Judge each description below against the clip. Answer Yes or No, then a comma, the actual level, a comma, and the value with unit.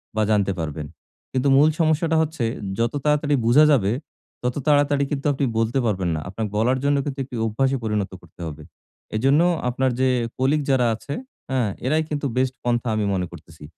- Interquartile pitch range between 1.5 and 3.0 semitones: No, average, 4.9 semitones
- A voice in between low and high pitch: No, low, 130 Hz